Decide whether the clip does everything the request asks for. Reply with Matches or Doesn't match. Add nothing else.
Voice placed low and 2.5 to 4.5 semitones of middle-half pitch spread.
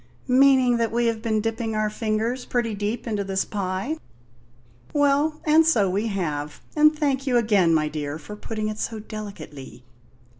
Doesn't match